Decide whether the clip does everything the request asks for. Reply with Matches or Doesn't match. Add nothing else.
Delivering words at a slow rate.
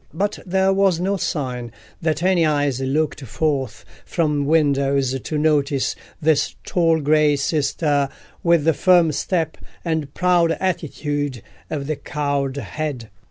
Matches